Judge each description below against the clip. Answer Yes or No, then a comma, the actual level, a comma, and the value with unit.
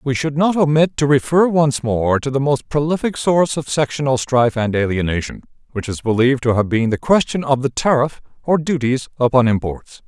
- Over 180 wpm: Yes, average, 195 wpm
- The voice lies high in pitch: No, low, 135 Hz